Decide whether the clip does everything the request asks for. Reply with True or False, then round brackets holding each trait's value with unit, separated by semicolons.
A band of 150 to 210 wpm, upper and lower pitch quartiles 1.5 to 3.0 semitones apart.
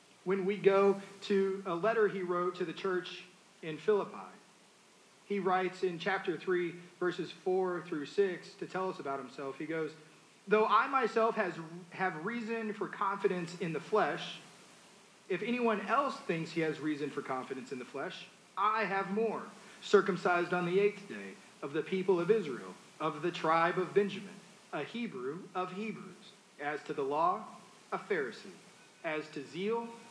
True (165 wpm; 2.7 semitones)